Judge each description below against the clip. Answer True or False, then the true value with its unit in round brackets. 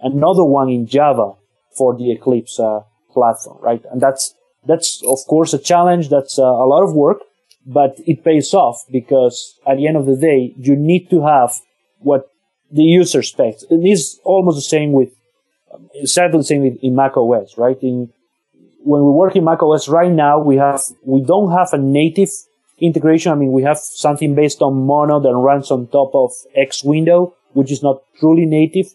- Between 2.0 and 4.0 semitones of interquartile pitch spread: True (3.6 semitones)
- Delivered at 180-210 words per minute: True (195 wpm)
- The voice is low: False (145 Hz)